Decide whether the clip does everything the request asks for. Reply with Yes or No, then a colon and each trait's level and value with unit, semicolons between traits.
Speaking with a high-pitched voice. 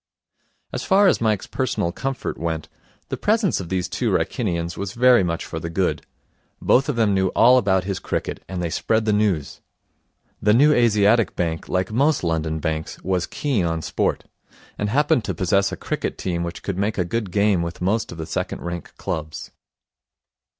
No: very low, 95 Hz